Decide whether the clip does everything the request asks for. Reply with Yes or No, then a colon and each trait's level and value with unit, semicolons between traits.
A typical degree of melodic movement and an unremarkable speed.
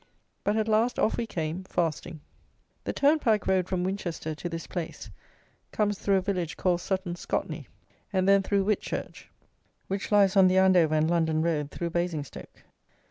Yes: average, 3.0 semitones; average, 165 wpm